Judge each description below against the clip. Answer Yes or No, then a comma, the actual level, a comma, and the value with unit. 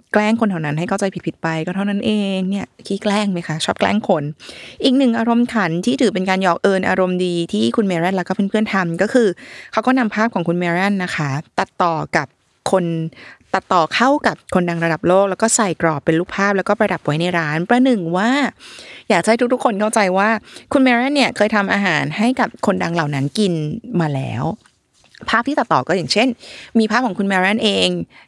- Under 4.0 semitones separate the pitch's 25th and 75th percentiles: No, average, 4.7 semitones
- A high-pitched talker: Yes, high, 195 Hz